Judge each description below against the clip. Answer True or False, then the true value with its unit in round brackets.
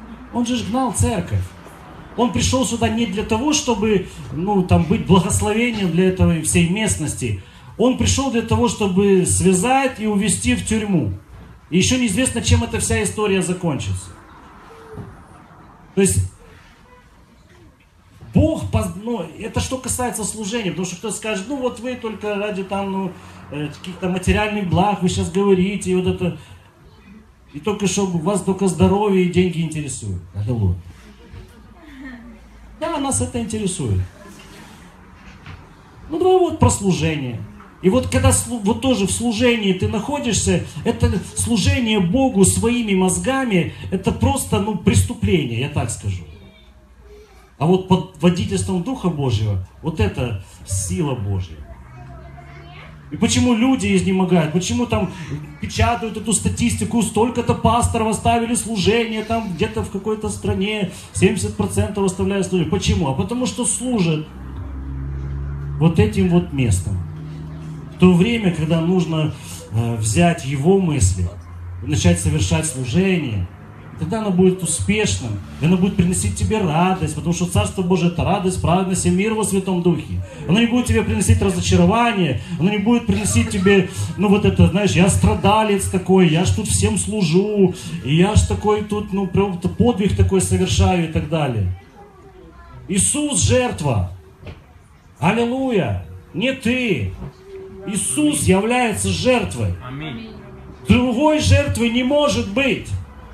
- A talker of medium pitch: True (180 Hz)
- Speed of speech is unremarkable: True (135 wpm)